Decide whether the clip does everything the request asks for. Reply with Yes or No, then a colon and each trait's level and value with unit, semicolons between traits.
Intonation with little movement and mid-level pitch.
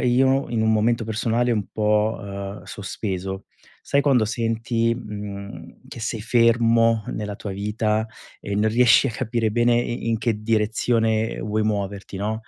No: narrow, 1.9 semitones; low, 110 Hz